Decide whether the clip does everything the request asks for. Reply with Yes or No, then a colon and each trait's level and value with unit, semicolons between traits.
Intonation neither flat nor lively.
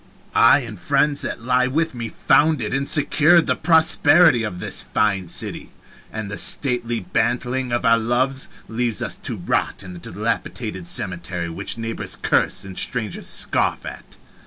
Yes: average, 4.6 semitones